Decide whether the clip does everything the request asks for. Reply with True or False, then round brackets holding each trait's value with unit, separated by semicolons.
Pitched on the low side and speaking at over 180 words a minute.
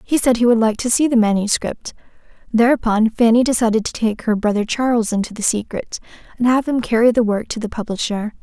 False (225 Hz; 205 wpm)